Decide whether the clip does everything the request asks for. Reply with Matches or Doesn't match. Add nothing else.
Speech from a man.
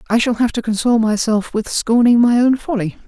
Doesn't match